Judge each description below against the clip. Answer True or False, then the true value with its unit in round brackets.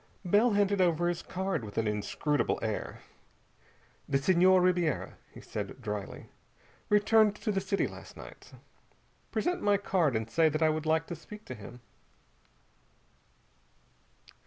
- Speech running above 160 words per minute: False (140 wpm)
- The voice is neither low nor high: True (170 Hz)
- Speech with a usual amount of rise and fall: False (7.4 semitones)